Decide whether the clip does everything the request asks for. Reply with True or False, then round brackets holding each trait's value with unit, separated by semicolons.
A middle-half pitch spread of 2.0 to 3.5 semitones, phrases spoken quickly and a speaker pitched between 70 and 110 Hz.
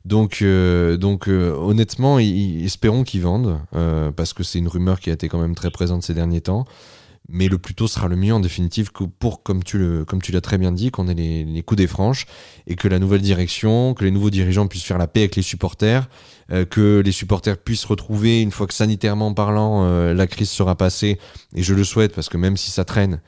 True (3.1 semitones; 245 wpm; 95 Hz)